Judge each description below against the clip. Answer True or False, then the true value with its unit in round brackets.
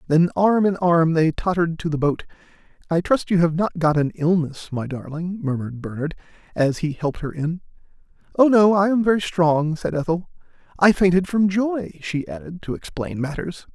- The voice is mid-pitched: True (170 Hz)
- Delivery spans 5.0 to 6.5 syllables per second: True (5.2 syllables/s)